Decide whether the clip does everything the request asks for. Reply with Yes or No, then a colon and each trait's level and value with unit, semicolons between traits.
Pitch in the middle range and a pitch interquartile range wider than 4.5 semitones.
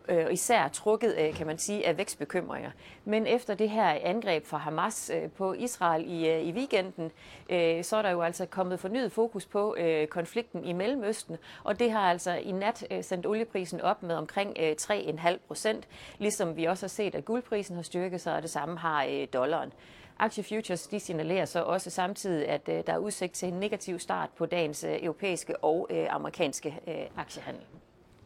No: medium, 180 Hz; average, 3.9 semitones